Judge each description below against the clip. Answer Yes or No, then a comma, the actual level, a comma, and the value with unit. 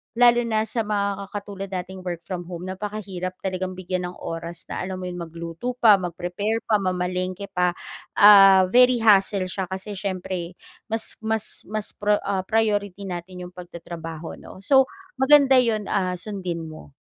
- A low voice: No, high, 190 Hz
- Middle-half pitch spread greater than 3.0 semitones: No, narrow, 2.6 semitones